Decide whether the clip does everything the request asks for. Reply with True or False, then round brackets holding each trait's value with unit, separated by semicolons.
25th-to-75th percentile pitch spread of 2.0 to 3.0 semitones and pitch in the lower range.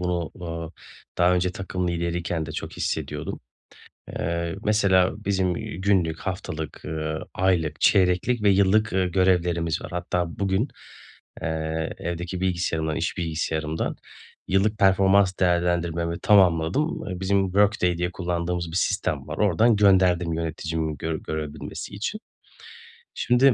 True (2.6 semitones; 90 Hz)